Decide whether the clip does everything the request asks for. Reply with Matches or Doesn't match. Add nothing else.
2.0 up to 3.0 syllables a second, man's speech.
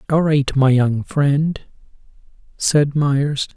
Matches